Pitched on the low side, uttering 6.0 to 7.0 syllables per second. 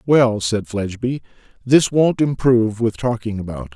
No: low, 115 Hz; 4.8 syllables/s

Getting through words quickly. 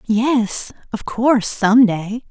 No: slow, 105 wpm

